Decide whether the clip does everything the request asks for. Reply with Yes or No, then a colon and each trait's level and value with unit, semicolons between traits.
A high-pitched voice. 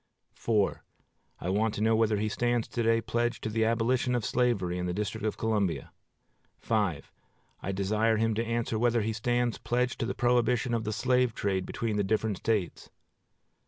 No: low, 110 Hz